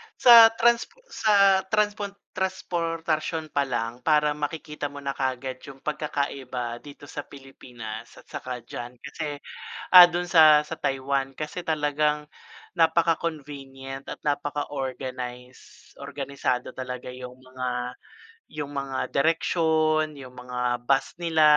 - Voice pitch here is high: No, medium, 145 Hz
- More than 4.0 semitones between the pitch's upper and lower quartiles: No, average, 3.5 semitones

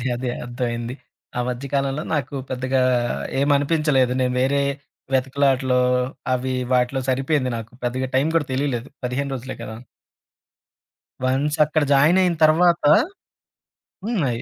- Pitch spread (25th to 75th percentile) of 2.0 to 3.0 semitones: Yes, narrow, 2.4 semitones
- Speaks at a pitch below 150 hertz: Yes, low, 135 Hz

